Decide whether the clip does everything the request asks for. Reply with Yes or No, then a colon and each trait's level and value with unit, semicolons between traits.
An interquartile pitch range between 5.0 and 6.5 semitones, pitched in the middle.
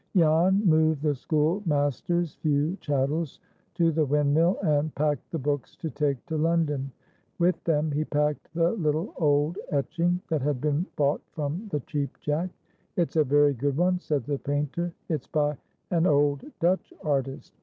No: narrow, 2.5 semitones; medium, 150 Hz